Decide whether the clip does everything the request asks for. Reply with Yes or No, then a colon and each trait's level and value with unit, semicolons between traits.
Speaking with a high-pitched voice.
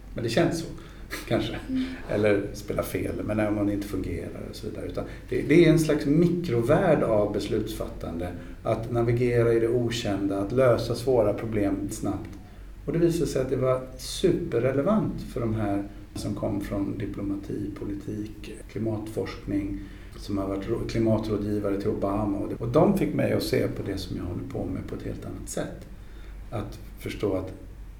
No: low, 105 Hz